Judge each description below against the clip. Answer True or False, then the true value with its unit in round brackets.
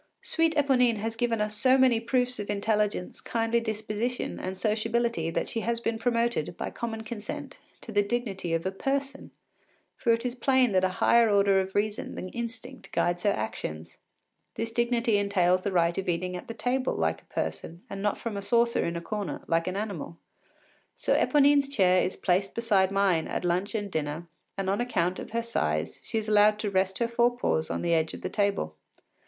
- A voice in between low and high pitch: False (210 Hz)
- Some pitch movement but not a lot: True (4.1 semitones)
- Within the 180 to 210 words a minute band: True (200 wpm)